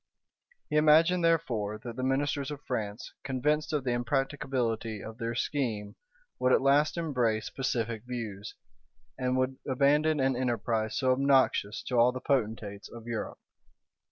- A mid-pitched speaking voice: No, low, 130 Hz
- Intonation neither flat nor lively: Yes, average, 3.5 semitones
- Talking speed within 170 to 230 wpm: No, average, 145 wpm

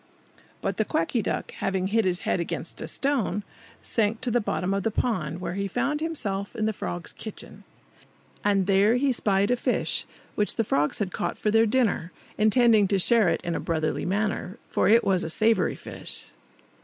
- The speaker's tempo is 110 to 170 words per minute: No, average, 190 wpm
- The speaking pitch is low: No, high, 205 Hz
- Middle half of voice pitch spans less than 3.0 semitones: No, average, 3.3 semitones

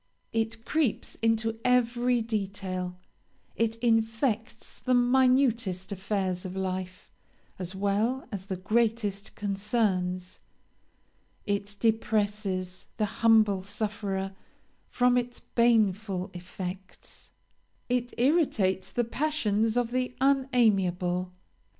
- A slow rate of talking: Yes, slow, 95 wpm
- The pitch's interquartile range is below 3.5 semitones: No, average, 3.8 semitones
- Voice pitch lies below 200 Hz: No, high, 215 Hz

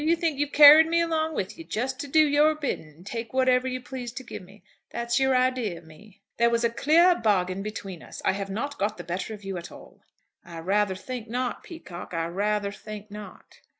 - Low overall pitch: No, high, 235 Hz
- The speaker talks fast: Yes, fast, 225 wpm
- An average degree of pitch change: No, wide, 6.0 semitones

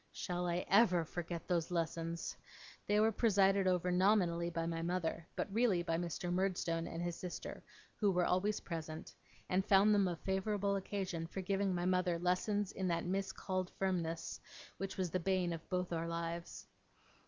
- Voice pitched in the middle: Yes, medium, 180 Hz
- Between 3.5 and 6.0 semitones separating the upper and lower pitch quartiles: No, narrow, 2.4 semitones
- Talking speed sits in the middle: Yes, average, 170 wpm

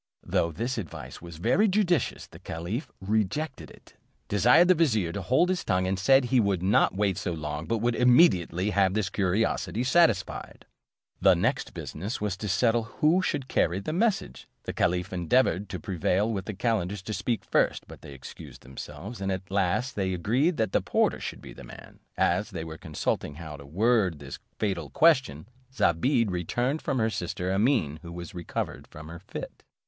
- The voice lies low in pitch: Yes, low, 100 Hz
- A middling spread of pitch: No, wide, 5.9 semitones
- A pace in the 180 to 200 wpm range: Yes, average, 185 wpm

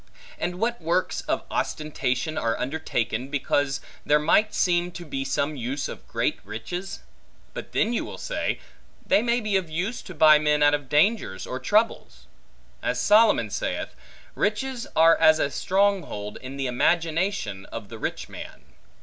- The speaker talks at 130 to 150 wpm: No, average, 165 wpm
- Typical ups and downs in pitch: No, wide, 6.5 semitones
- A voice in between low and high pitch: Yes, medium, 155 Hz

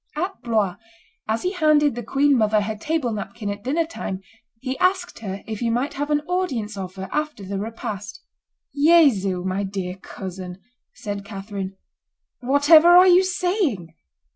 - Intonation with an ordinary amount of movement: No, wide, 7.4 semitones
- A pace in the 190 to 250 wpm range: No, average, 160 wpm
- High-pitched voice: Yes, high, 230 Hz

